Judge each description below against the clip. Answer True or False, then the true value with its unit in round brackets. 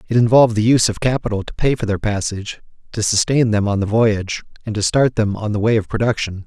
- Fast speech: True (240 wpm)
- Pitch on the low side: True (110 Hz)